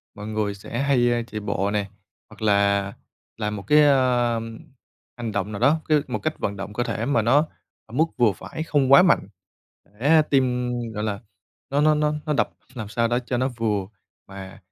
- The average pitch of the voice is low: Yes, low, 120 Hz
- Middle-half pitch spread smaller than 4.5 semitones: No, average, 4.8 semitones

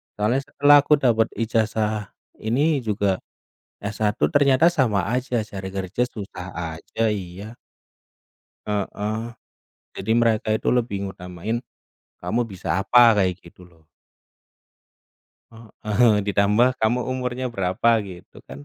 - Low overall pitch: Yes, low, 110 Hz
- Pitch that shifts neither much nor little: Yes, average, 3.6 semitones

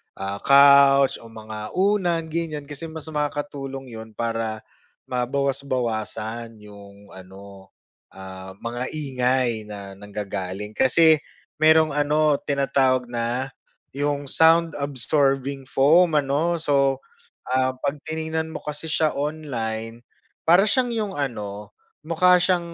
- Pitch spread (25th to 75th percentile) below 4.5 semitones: No, wide, 5.5 semitones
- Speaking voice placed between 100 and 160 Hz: Yes, low, 135 Hz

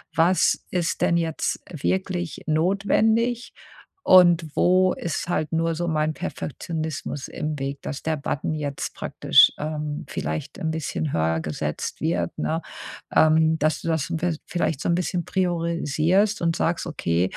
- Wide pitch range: No, narrow, 2.5 semitones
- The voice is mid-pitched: Yes, medium, 160 Hz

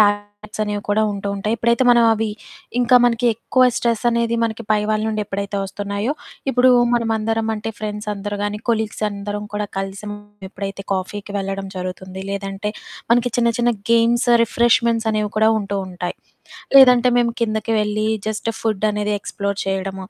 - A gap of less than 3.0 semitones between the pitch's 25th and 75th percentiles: Yes, narrow, 2.5 semitones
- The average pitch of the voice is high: Yes, high, 215 Hz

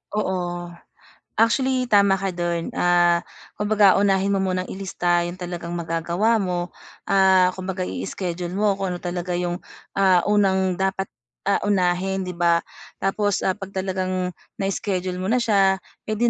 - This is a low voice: No, high, 190 Hz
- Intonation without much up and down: Yes, narrow, 1.9 semitones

